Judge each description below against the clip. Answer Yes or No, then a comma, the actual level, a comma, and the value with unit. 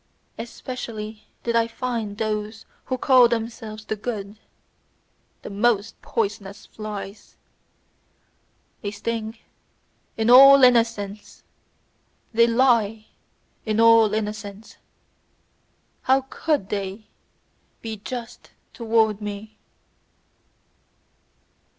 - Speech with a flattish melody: Yes, narrow, 1.9 semitones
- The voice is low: No, high, 220 Hz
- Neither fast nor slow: No, slow, 85 wpm